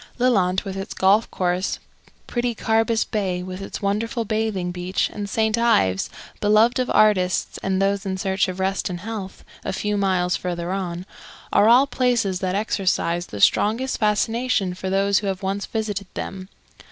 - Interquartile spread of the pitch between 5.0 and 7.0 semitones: No, average, 2.9 semitones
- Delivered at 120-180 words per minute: Yes, average, 165 wpm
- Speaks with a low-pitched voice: No, high, 195 Hz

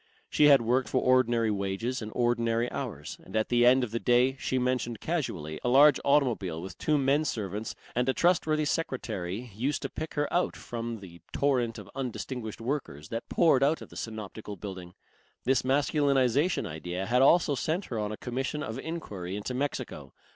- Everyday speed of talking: Yes, average, 180 wpm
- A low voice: Yes, low, 125 Hz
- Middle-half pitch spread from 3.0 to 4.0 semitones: No, average, 4.4 semitones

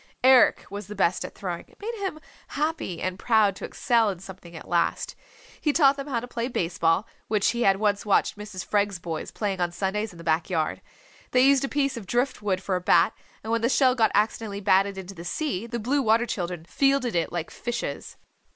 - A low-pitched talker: No, high, 210 Hz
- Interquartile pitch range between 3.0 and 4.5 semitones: No, average, 4.9 semitones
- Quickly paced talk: Yes, fast, 225 wpm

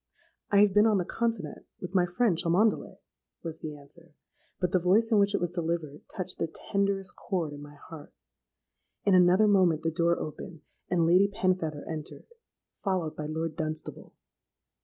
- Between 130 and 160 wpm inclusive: No, average, 170 wpm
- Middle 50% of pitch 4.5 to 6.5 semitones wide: No, average, 3.6 semitones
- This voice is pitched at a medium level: Yes, medium, 175 Hz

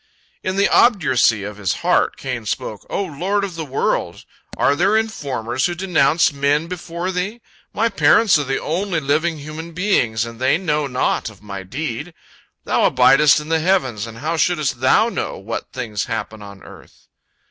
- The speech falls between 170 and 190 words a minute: Yes, average, 175 wpm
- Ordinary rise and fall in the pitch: No, wide, 6.9 semitones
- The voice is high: No, medium, 150 Hz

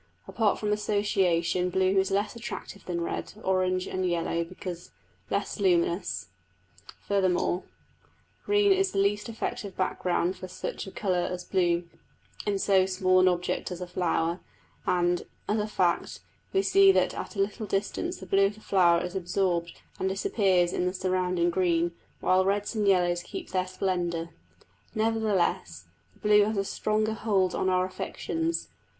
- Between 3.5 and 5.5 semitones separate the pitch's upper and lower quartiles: No, narrow, 2.5 semitones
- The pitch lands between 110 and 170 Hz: No, medium, 185 Hz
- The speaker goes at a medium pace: Yes, average, 160 wpm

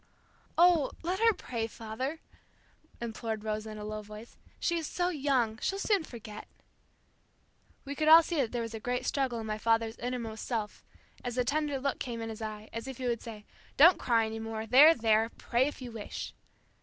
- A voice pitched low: No, high, 235 Hz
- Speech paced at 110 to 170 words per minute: No, average, 200 wpm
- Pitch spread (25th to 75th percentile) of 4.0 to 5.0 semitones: Yes, average, 4.3 semitones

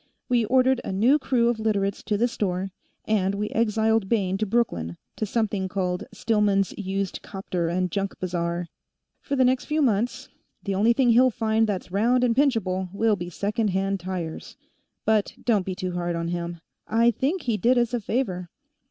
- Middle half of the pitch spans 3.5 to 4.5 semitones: Yes, average, 3.9 semitones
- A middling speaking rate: Yes, average, 185 wpm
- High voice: Yes, high, 205 Hz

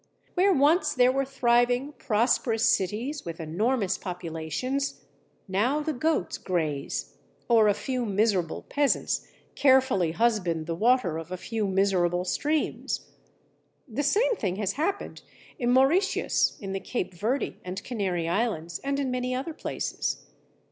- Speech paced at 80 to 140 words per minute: Yes, slow, 135 wpm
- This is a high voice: Yes, high, 230 Hz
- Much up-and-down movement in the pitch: Yes, wide, 6.7 semitones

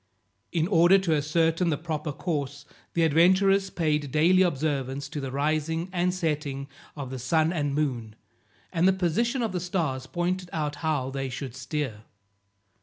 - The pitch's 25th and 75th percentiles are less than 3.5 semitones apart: No, average, 3.8 semitones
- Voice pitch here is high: No, medium, 155 Hz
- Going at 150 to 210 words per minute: Yes, average, 160 wpm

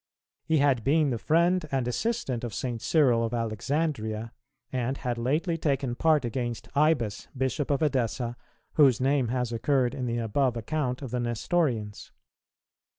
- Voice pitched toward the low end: Yes, low, 130 Hz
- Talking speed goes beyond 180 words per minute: No, average, 155 wpm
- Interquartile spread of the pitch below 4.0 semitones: Yes, average, 3.6 semitones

